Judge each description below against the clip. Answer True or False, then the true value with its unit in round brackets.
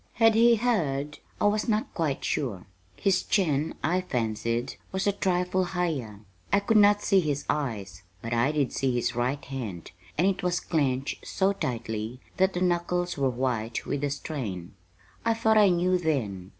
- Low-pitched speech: False (150 Hz)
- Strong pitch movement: True (7.5 semitones)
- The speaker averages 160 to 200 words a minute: True (175 wpm)